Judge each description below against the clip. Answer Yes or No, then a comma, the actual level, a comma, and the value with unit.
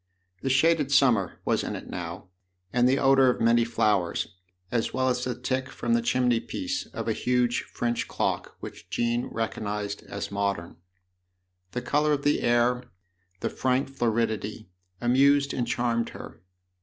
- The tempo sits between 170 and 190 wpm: No, average, 155 wpm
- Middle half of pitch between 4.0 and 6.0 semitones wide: No, average, 2.7 semitones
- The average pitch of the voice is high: No, low, 125 Hz